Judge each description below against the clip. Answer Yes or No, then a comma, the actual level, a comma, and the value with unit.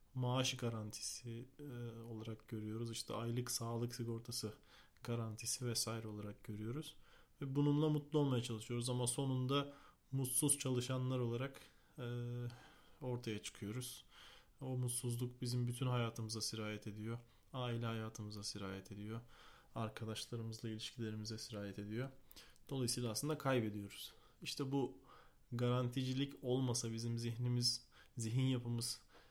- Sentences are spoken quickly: No, average, 105 wpm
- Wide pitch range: No, narrow, 2.5 semitones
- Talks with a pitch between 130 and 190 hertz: No, low, 120 Hz